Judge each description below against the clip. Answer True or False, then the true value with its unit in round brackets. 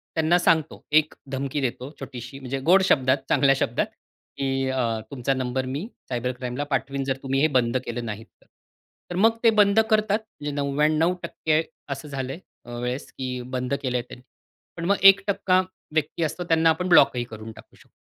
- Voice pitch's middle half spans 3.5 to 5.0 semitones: True (4.1 semitones)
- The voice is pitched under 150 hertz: True (140 Hz)